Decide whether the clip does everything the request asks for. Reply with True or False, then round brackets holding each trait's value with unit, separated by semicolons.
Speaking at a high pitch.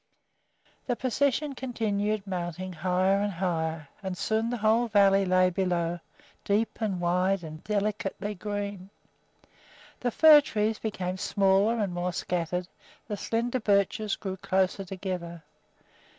True (195 Hz)